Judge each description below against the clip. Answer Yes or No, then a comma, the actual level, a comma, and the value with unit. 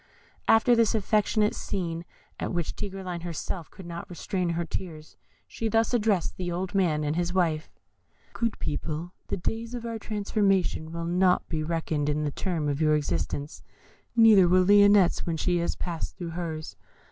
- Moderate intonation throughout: Yes, average, 3.9 semitones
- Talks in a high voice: No, medium, 175 Hz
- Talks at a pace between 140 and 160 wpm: No, average, 170 wpm